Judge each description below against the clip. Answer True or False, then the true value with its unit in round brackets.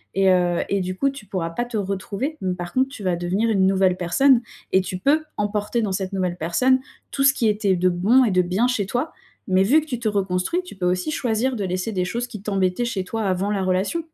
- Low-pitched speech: False (200 Hz)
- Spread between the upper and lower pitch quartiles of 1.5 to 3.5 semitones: False (4.6 semitones)